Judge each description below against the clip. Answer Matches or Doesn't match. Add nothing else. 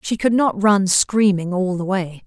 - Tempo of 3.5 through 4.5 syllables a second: Matches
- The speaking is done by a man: Doesn't match